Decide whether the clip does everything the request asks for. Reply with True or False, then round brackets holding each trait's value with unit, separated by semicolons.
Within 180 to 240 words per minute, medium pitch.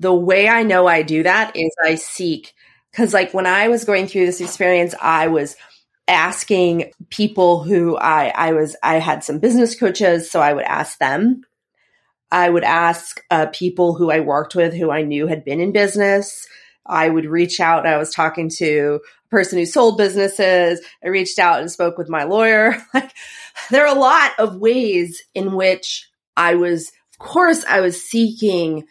True (185 wpm; 180 Hz)